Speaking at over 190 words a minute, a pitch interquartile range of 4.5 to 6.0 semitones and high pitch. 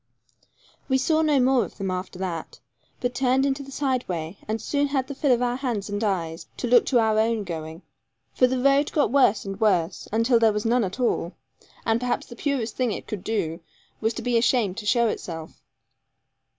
Yes: fast, 205 wpm; average, 4.8 semitones; high, 230 Hz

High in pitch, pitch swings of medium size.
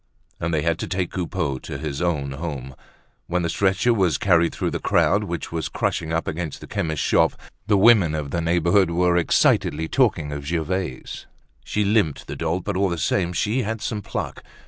No: very low, 85 Hz; average, 3.4 semitones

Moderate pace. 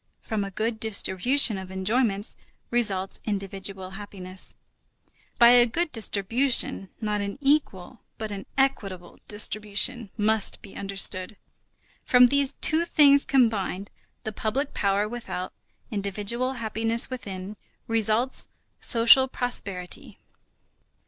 No: slow, 110 wpm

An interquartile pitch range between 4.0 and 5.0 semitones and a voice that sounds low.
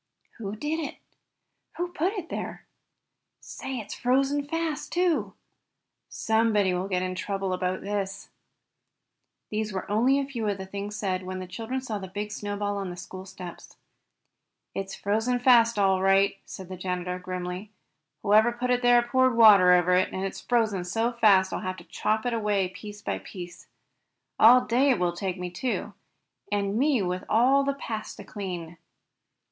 No: average, 4.4 semitones; high, 205 Hz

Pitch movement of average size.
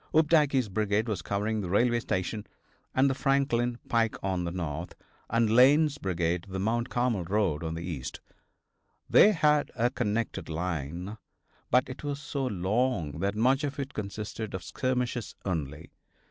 No: wide, 5.9 semitones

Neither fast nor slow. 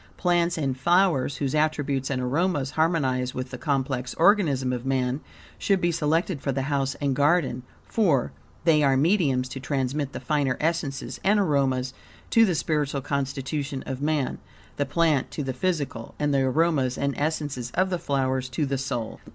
Yes: average, 170 wpm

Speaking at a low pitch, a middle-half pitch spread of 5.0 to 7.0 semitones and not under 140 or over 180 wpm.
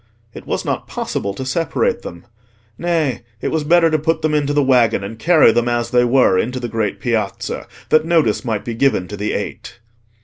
No: low, 125 Hz; wide, 5.6 semitones; fast, 205 wpm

